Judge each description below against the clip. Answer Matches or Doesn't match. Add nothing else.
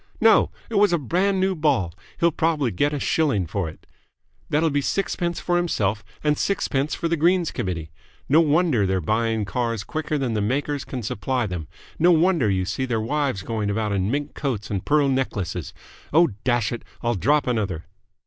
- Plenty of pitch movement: Matches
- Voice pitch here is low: Matches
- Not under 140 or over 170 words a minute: Doesn't match